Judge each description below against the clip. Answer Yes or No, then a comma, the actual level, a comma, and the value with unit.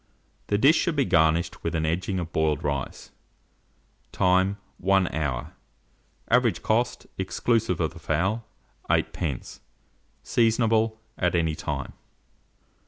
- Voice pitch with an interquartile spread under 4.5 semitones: No, wide, 5.6 semitones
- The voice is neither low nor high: No, very low, 90 Hz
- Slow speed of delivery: Yes, slow, 115 wpm